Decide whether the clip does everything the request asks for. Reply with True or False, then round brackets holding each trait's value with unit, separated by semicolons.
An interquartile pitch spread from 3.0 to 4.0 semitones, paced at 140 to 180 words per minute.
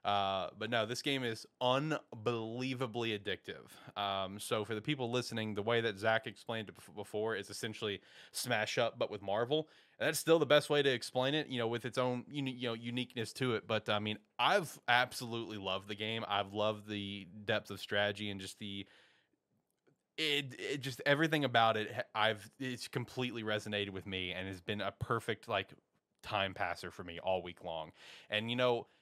False (3.6 semitones; 190 wpm)